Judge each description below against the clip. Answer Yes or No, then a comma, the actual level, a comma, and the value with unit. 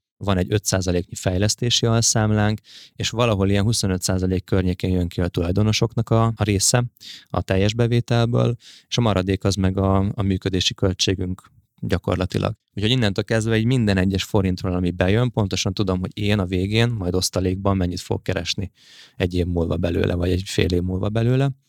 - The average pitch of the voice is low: Yes, low, 100 Hz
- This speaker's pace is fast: Yes, fast, 165 wpm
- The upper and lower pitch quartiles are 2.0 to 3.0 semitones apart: No, average, 3.4 semitones